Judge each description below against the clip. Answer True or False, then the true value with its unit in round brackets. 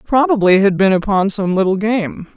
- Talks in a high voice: True (200 Hz)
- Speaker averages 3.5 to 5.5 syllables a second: True (5.1 syllables/s)